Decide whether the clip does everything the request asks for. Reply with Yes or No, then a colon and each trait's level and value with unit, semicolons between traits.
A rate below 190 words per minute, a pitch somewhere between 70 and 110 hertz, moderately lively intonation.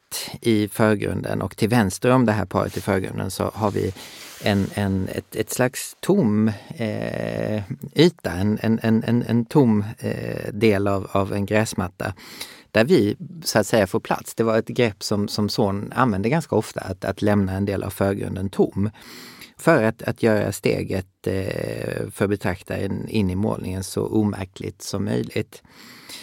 No: average, 165 wpm; low, 105 Hz; narrow, 2.2 semitones